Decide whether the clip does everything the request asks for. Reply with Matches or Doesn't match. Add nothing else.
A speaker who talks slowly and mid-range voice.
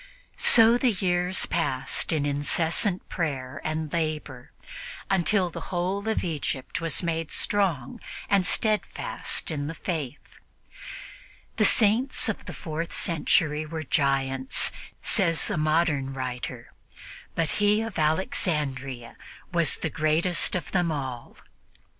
Matches